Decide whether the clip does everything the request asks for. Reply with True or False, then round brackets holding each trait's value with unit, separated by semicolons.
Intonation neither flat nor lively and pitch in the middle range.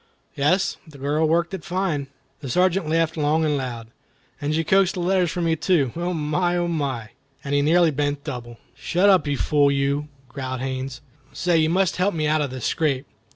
True (3.7 semitones; 155 Hz)